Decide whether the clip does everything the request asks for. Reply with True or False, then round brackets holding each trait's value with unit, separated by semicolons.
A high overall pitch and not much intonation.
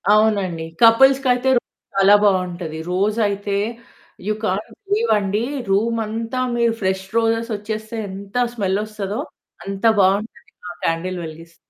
False (205 Hz; 3.0 semitones)